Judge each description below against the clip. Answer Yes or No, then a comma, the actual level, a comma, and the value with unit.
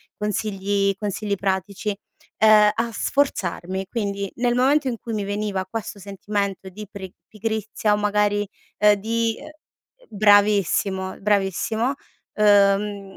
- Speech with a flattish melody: Yes, narrow, 1.7 semitones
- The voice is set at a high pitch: Yes, high, 205 Hz